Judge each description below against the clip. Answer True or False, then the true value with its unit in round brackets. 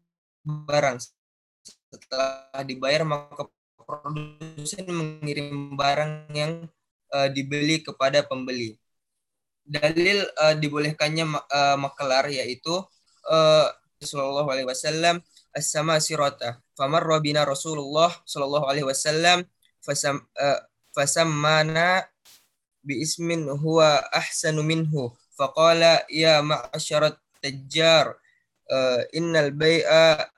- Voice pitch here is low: False (150 Hz)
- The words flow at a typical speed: True (95 wpm)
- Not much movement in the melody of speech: True (2.3 semitones)